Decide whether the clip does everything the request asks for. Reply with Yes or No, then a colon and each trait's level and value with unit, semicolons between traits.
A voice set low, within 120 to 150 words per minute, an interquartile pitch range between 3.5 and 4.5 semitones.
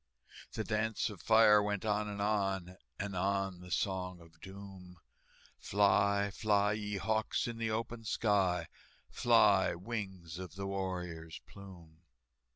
No: low, 100 Hz; slow, 135 wpm; narrow, 2.4 semitones